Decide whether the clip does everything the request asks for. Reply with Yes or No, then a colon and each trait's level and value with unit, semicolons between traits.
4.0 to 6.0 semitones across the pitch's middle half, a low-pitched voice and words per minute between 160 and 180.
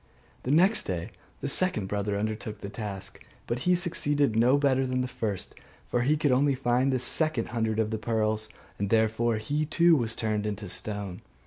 No: average, 4.4 semitones; low, 115 Hz; average, 190 wpm